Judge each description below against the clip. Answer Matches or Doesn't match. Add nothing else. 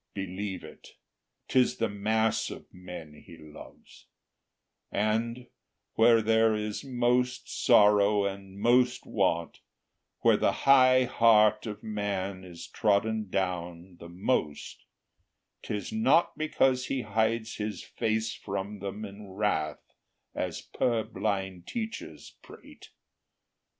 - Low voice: Matches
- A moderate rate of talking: Doesn't match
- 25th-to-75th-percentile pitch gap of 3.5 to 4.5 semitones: Doesn't match